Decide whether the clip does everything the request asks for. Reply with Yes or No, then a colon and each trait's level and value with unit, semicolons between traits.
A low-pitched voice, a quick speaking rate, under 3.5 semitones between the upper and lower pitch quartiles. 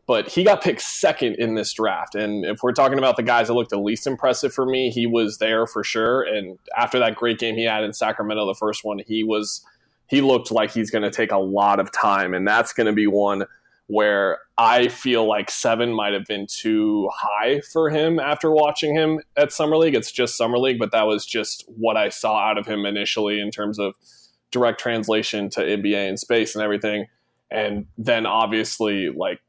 Yes: low, 110 Hz; fast, 215 wpm; average, 2.8 semitones